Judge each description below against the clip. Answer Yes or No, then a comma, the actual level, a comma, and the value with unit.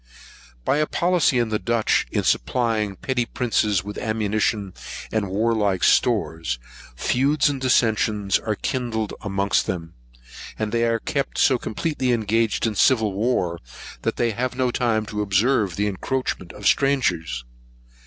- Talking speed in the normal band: Yes, average, 145 wpm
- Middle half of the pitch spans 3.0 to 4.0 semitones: Yes, average, 3.7 semitones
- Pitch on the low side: Yes, low, 110 Hz